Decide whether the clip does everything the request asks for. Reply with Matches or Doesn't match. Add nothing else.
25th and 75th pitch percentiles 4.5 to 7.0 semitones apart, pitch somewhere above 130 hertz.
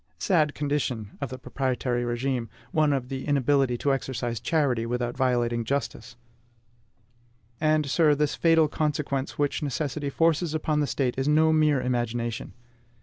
Doesn't match